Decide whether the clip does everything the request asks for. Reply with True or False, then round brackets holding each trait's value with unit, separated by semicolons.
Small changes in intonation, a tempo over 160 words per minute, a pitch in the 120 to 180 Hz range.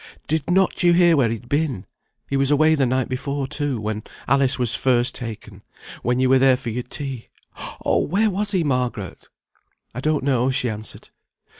False (3.3 semitones; 185 wpm; 135 Hz)